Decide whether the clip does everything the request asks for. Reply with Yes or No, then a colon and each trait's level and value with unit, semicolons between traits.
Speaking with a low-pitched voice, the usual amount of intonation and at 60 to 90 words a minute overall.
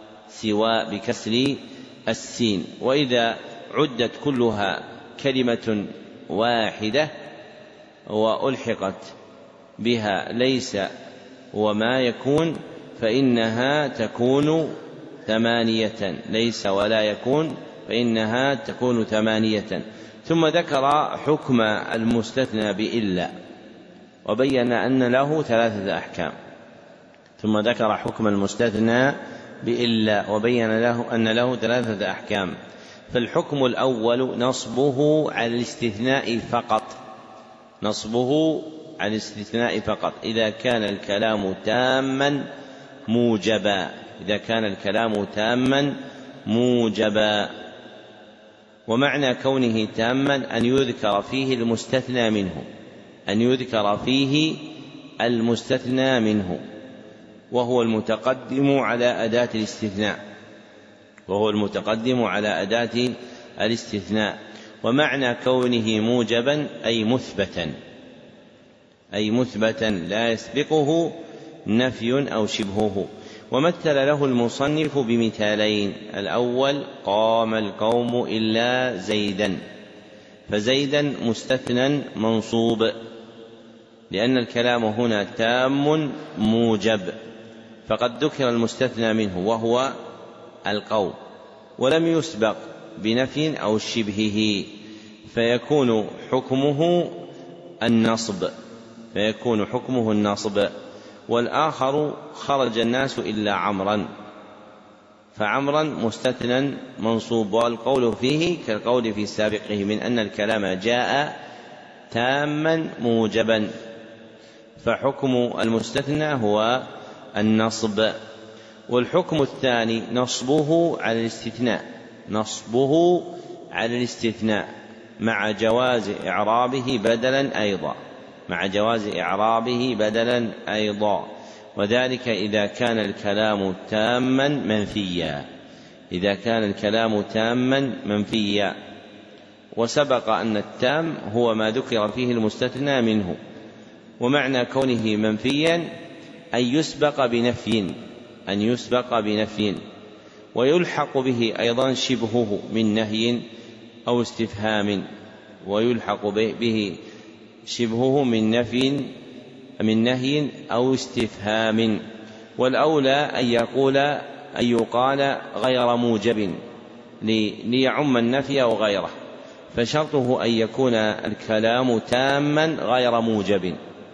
Yes: low, 115 Hz; average, 3.0 semitones; average, 80 wpm